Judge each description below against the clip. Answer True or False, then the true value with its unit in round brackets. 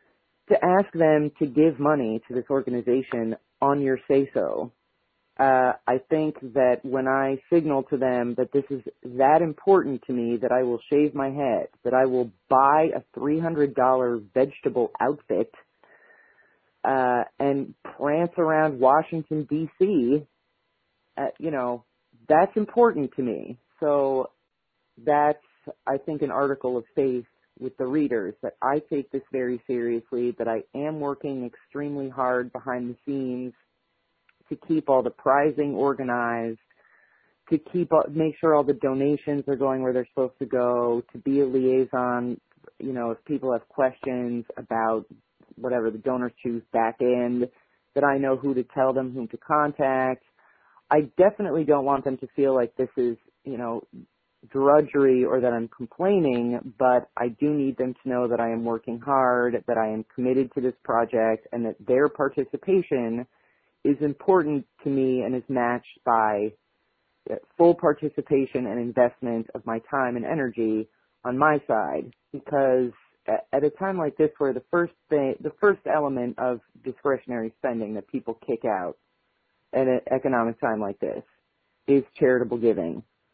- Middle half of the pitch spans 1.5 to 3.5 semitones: True (2.9 semitones)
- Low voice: True (130 Hz)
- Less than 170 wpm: True (160 wpm)